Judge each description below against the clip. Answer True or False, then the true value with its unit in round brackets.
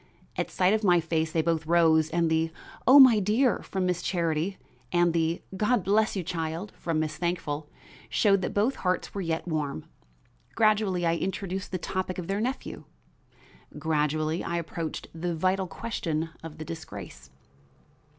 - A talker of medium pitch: True (170 Hz)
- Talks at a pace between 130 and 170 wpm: True (160 wpm)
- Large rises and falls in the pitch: False (3.3 semitones)